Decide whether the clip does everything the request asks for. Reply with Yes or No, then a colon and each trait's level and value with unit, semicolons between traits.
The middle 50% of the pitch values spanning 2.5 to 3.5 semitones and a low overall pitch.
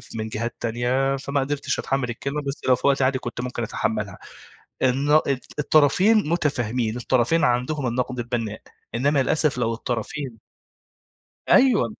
Yes: average, 3.2 semitones; low, 130 Hz